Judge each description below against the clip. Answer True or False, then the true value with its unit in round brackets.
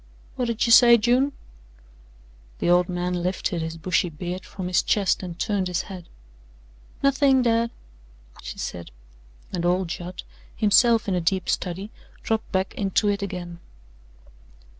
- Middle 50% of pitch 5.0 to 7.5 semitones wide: False (4.1 semitones)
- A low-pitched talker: False (190 Hz)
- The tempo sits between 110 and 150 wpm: True (140 wpm)